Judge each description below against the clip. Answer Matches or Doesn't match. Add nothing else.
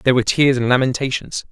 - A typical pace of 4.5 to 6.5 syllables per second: Doesn't match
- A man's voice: Matches